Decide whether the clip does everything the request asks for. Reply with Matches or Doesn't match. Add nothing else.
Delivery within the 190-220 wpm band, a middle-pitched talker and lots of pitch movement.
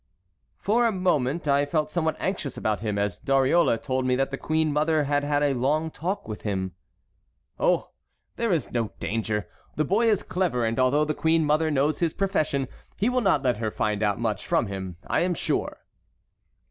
Matches